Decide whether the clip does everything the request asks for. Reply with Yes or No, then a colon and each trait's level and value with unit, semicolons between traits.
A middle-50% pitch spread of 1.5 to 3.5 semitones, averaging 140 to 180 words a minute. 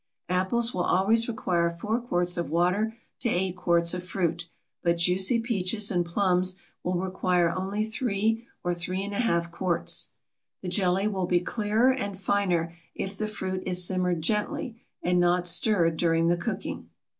Yes: average, 3.1 semitones; average, 155 wpm